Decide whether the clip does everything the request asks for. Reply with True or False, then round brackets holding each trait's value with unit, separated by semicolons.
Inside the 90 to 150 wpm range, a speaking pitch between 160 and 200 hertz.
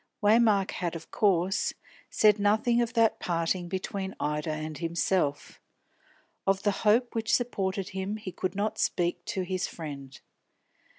True (140 wpm; 190 Hz)